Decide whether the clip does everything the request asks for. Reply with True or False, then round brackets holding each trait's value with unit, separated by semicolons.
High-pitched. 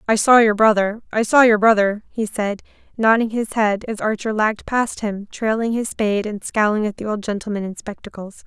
True (215 Hz)